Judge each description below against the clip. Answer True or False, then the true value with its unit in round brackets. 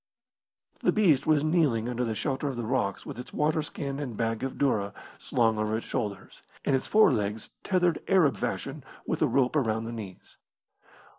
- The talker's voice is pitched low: True (125 Hz)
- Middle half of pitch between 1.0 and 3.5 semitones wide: False (4.9 semitones)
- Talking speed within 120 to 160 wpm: False (175 wpm)